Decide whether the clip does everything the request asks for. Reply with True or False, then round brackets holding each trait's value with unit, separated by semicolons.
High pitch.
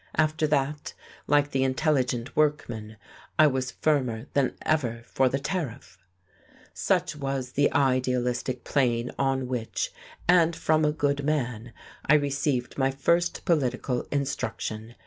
False (135 Hz)